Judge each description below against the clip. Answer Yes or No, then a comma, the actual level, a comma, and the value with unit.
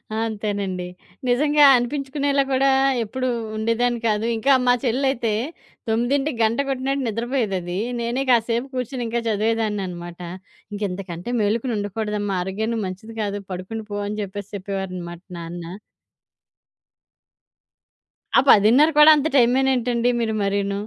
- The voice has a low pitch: No, high, 225 Hz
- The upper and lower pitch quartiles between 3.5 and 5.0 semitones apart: Yes, average, 4.0 semitones